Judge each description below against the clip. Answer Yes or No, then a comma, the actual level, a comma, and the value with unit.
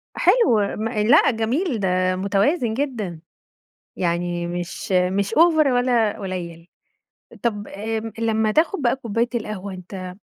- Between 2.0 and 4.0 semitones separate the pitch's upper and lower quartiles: No, average, 4.7 semitones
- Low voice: No, high, 215 Hz